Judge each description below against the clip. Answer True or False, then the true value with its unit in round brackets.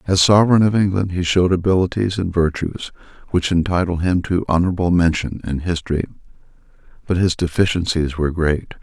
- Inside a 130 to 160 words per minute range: True (150 wpm)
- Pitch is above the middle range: False (90 Hz)